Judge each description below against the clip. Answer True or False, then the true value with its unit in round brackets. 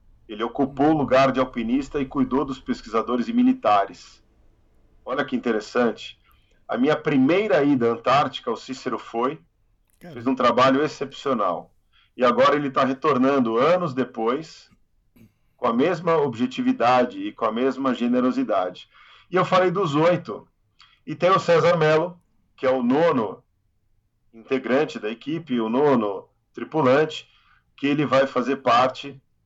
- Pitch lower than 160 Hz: True (135 Hz)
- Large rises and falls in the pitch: False (4.3 semitones)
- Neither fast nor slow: True (140 wpm)